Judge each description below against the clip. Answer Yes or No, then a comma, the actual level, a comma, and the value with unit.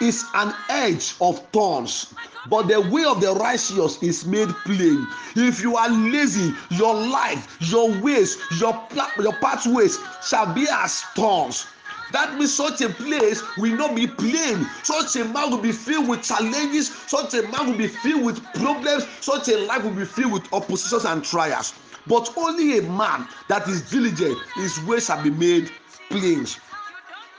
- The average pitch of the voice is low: No, high, 235 Hz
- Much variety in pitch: Yes, wide, 5.7 semitones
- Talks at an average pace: Yes, average, 170 wpm